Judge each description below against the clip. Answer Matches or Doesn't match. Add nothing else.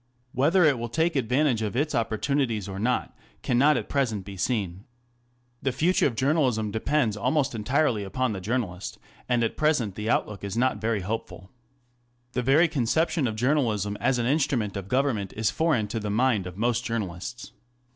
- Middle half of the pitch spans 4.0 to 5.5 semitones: Matches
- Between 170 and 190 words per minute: Matches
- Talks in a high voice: Doesn't match